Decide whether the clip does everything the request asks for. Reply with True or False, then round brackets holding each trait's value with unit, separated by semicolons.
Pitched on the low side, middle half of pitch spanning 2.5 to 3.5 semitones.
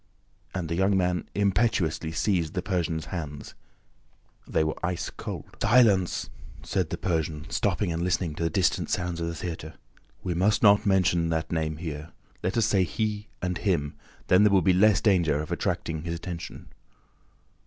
True (90 Hz; 3.1 semitones)